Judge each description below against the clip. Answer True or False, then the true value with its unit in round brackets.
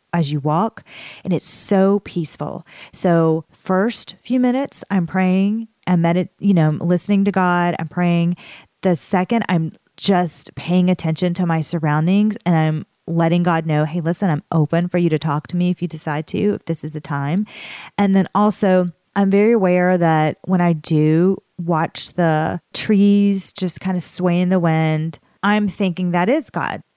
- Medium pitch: True (180 Hz)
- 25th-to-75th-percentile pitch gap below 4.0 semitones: True (3.2 semitones)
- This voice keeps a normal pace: True (180 wpm)